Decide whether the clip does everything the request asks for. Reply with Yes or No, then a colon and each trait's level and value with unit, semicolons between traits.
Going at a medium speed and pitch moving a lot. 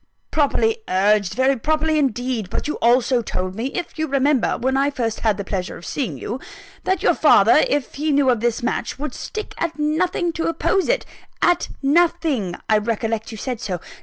Yes: average, 195 wpm; wide, 5.8 semitones